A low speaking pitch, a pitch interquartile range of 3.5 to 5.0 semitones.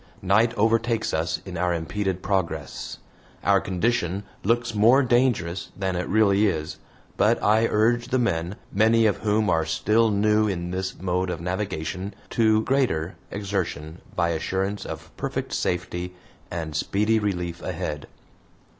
Yes: very low, 95 Hz; average, 3.9 semitones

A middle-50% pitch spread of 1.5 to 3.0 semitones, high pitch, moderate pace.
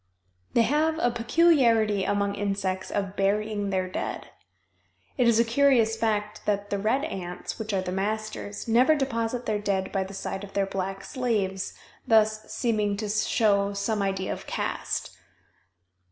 Yes: narrow, 2.6 semitones; high, 210 Hz; average, 155 wpm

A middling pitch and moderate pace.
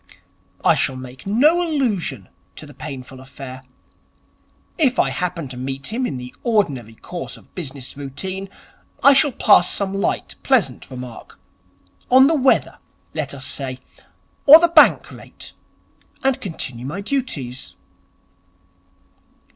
No: medium, 160 Hz; slow, 130 wpm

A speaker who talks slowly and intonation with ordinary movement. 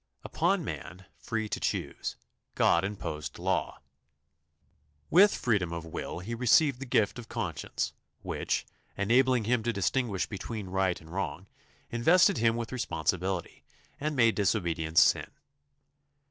Yes: slow, 130 wpm; average, 5.0 semitones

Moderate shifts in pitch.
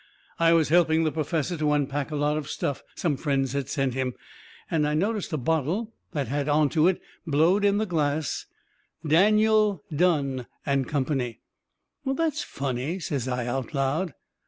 Yes: average, 3.9 semitones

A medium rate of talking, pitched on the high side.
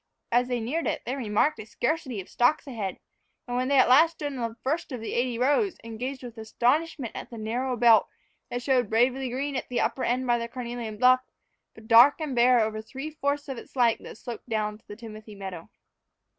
No: fast, 225 wpm; high, 245 Hz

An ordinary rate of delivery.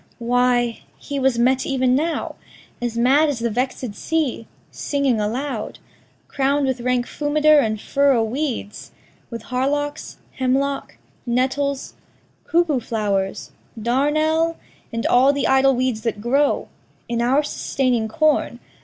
No: slow, 125 wpm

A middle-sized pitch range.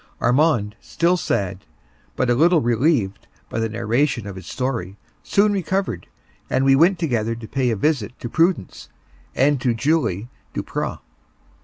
No: wide, 6.1 semitones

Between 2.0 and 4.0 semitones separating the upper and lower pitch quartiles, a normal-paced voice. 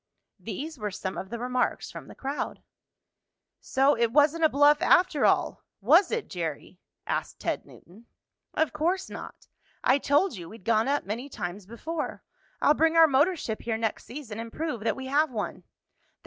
No: wide, 5.6 semitones; average, 175 wpm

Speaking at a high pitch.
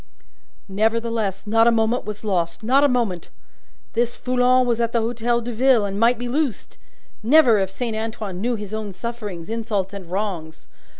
Yes: high, 225 Hz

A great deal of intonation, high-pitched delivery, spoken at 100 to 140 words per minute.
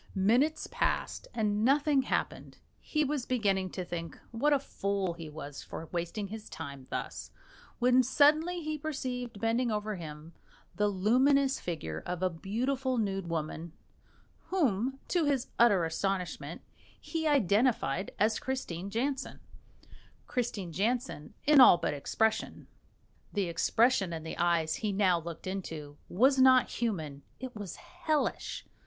Yes: wide, 7.0 semitones; high, 210 Hz; slow, 135 wpm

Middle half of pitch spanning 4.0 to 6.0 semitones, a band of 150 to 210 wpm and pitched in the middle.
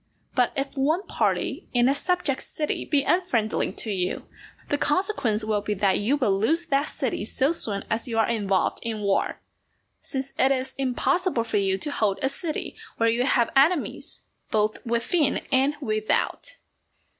No: average, 5.1 semitones; average, 170 wpm; very high, 255 Hz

